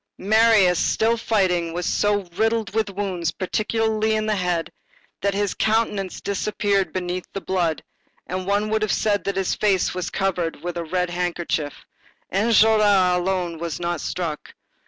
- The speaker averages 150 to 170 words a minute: Yes, average, 155 wpm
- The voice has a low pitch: No, high, 195 Hz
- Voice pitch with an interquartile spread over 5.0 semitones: No, average, 3.1 semitones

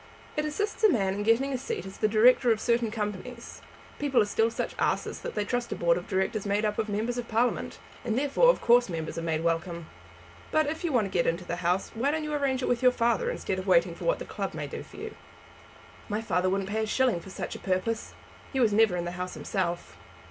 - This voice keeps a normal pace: No, fast, 250 wpm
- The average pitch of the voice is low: No, high, 220 Hz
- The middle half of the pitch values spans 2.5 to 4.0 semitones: No, average, 4.9 semitones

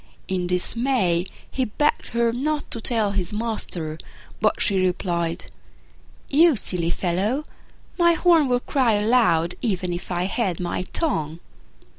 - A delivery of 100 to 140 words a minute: Yes, slow, 135 wpm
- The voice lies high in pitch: Yes, high, 205 Hz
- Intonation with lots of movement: Yes, wide, 6.0 semitones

